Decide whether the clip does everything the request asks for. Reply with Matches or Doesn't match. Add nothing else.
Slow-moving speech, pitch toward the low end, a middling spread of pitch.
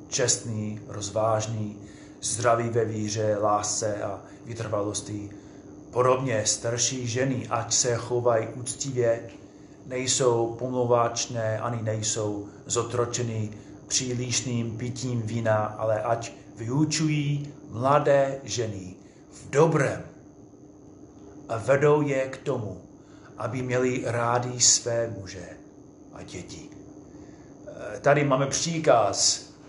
Matches